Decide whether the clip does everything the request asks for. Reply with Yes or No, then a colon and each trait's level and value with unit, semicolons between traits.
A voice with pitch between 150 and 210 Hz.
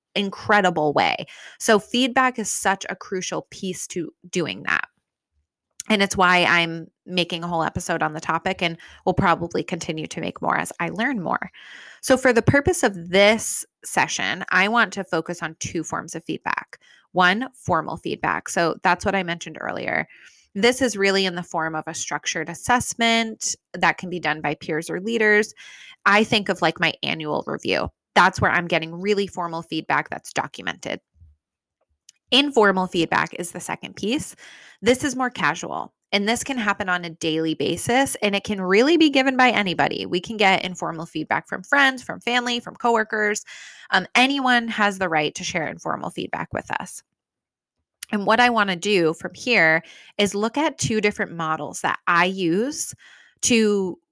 Yes: high, 190 Hz